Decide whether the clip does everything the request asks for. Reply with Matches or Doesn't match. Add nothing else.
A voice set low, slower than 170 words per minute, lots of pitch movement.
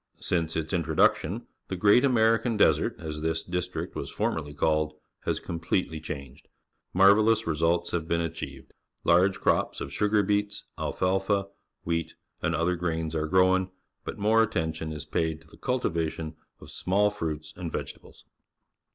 Doesn't match